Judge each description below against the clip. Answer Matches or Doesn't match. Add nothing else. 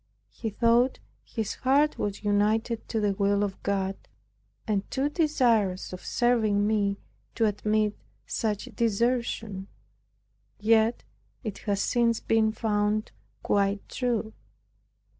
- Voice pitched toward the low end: Doesn't match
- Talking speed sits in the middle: Doesn't match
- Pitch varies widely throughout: Doesn't match